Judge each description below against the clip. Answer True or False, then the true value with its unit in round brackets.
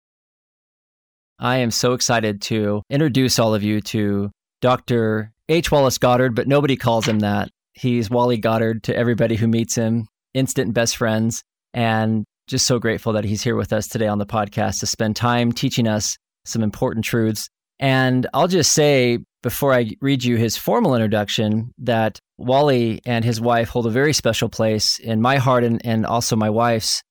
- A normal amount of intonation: False (2.3 semitones)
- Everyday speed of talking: True (175 wpm)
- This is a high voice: False (115 Hz)